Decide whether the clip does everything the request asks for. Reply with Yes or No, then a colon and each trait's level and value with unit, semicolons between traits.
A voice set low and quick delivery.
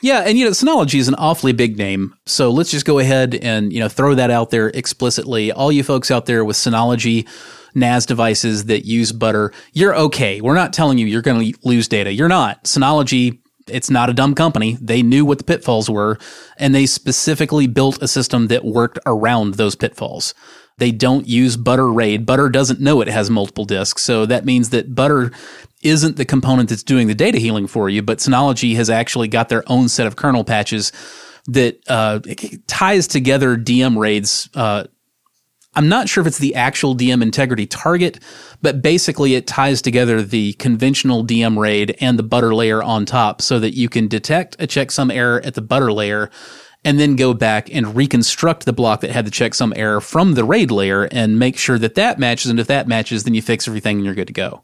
Yes: low, 120 Hz; fast, 210 wpm